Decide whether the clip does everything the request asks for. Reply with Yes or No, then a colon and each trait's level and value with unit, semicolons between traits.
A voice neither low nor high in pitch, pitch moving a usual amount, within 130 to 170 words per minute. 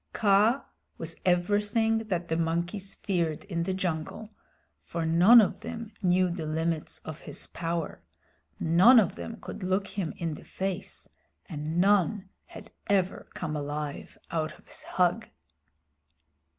Yes: medium, 180 Hz; average, 3.7 semitones; average, 140 wpm